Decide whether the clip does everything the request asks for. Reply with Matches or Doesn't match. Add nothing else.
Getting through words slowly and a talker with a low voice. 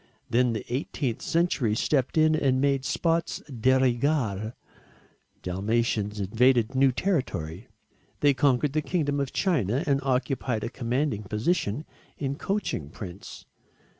Matches